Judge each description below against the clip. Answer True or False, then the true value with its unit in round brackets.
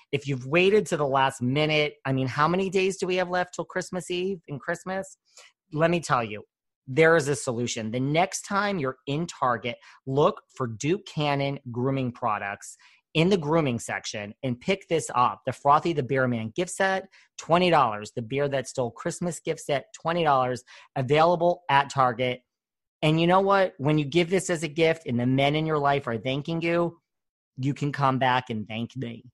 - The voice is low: False (145 Hz)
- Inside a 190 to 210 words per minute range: True (195 wpm)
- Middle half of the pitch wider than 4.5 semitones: True (4.9 semitones)